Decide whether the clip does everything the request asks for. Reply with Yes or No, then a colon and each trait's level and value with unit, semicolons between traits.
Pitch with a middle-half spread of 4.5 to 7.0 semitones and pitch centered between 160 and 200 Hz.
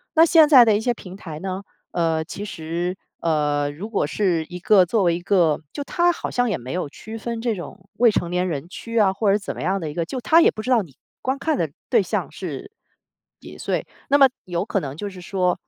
Yes: average, 5.1 semitones; high, 190 Hz